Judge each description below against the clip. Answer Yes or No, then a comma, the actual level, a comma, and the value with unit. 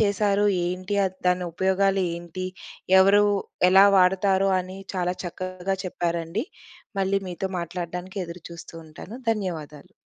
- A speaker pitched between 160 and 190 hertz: Yes, medium, 185 Hz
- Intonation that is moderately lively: No, narrow, 1.9 semitones